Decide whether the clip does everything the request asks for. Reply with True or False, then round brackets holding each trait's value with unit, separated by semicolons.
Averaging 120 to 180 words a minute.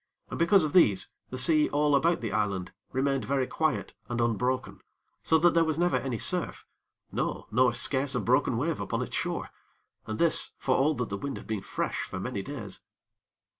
False (195 wpm)